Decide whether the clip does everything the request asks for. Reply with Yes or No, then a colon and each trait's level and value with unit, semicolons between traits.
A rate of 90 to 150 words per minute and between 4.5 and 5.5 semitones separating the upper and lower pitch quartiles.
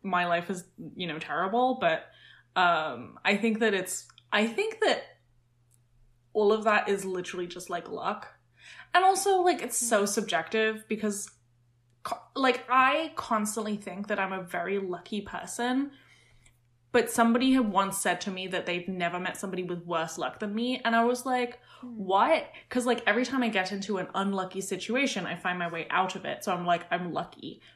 No: average, 180 wpm; average, 5.1 semitones